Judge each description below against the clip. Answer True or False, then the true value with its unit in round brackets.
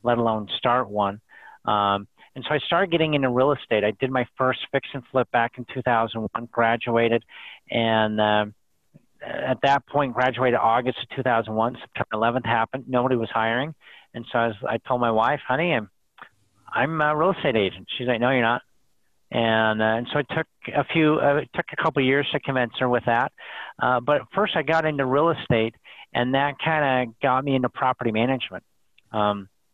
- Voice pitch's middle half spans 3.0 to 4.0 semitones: True (3.4 semitones)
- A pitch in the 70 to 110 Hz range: False (125 Hz)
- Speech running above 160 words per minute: True (200 wpm)